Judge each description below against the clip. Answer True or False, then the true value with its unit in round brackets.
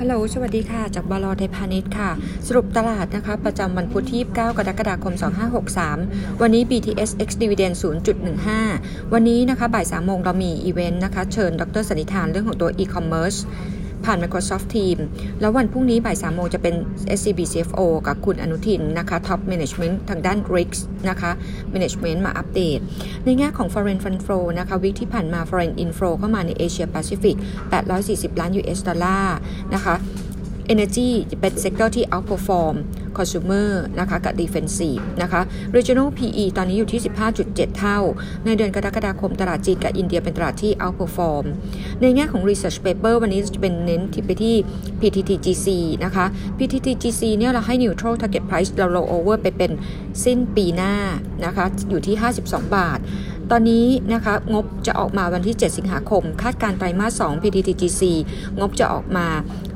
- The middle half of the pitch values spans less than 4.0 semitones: True (3.5 semitones)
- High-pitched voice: True (195 Hz)